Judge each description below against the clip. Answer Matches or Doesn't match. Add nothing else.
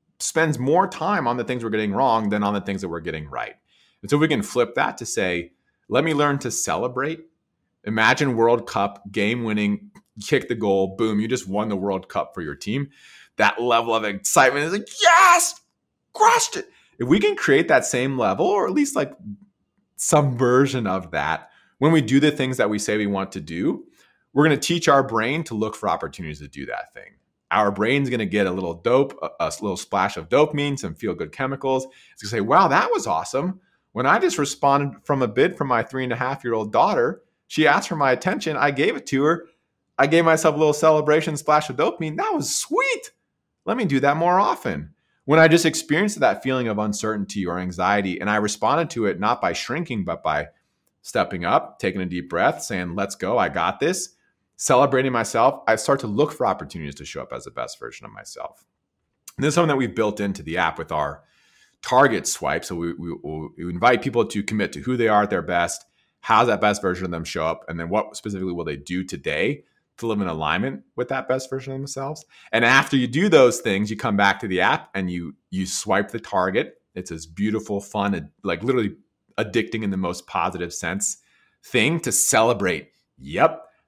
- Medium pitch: Doesn't match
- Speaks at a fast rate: Matches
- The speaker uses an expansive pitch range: Matches